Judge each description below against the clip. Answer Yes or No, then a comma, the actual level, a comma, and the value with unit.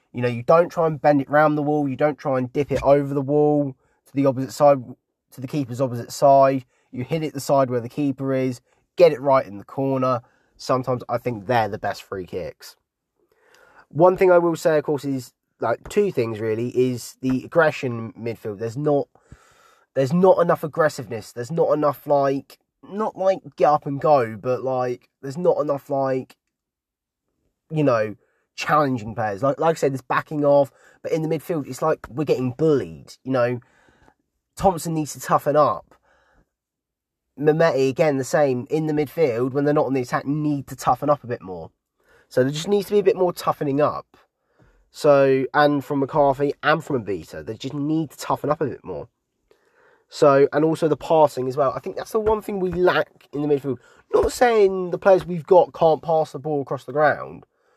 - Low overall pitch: No, medium, 145 Hz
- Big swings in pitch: No, average, 3.7 semitones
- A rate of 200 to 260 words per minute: Yes, fast, 205 wpm